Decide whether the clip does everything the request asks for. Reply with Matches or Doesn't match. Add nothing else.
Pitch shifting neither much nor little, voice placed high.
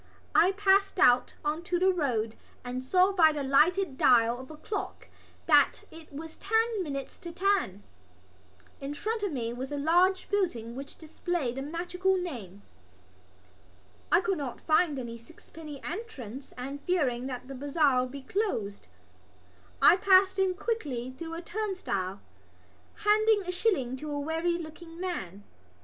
Doesn't match